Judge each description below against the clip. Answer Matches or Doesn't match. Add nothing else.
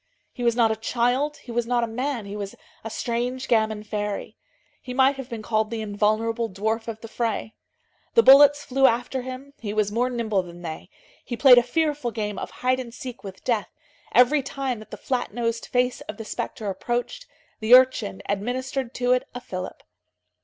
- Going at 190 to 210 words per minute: Matches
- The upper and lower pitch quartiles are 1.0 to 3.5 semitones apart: Matches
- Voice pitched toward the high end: Matches